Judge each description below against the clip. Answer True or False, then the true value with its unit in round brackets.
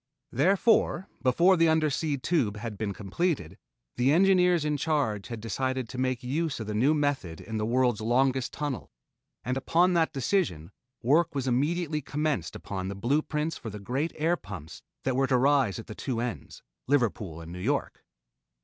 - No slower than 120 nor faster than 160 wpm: False (175 wpm)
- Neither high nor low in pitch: False (130 Hz)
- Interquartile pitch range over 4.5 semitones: True (5.6 semitones)